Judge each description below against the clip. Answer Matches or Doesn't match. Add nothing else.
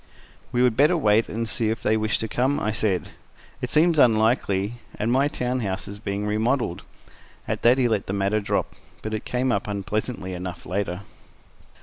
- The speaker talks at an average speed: Matches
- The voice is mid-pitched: Doesn't match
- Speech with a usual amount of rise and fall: Matches